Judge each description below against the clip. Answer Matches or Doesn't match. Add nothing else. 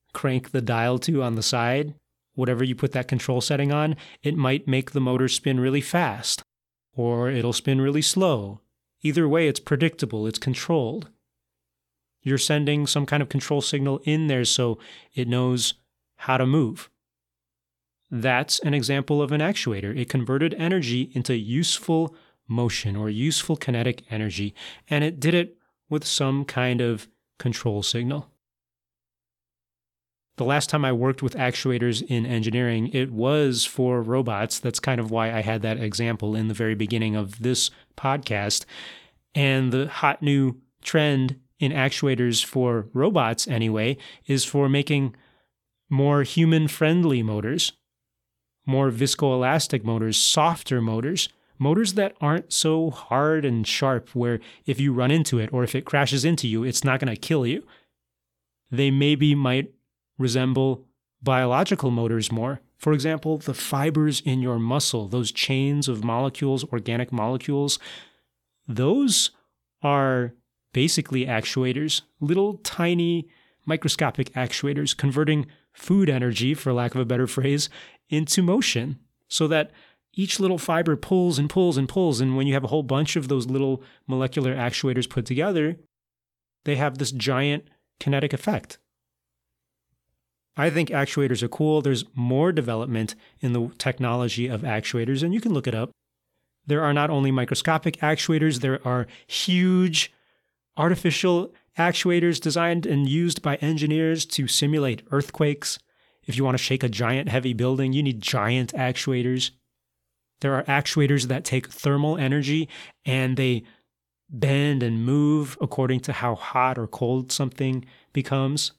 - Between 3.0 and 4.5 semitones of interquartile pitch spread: Matches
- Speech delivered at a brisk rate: Doesn't match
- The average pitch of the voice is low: Matches